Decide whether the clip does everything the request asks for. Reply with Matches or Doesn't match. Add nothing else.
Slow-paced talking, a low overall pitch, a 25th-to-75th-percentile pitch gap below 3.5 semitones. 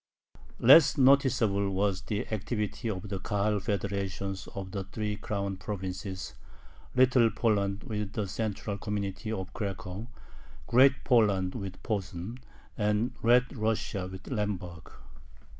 Matches